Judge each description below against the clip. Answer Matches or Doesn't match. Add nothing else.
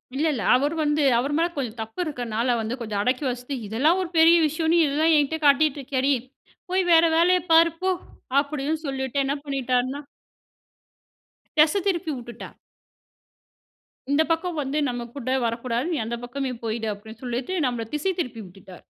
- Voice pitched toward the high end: Matches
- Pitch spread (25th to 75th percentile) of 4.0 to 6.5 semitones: Matches